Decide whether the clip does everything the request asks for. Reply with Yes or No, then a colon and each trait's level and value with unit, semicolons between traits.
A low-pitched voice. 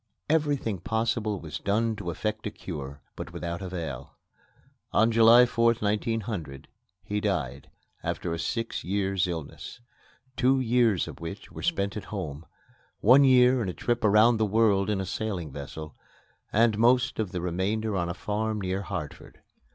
Yes: low, 105 Hz